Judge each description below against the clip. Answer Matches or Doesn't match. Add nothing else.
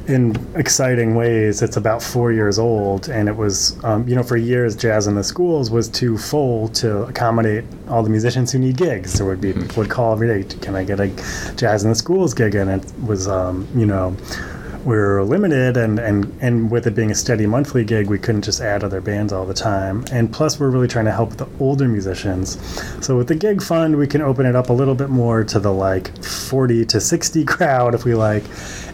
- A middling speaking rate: Doesn't match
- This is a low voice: Matches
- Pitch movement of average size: Matches